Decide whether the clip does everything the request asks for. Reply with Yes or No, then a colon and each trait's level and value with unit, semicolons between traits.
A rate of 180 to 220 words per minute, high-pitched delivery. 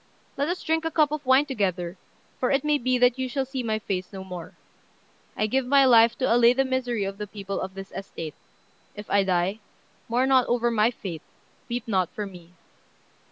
Yes: fast, 205 wpm; high, 235 Hz